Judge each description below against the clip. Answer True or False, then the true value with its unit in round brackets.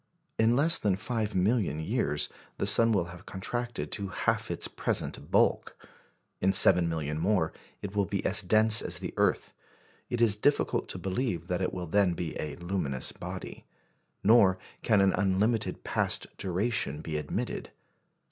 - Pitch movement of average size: True (4.1 semitones)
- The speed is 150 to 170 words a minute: True (160 wpm)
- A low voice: True (95 Hz)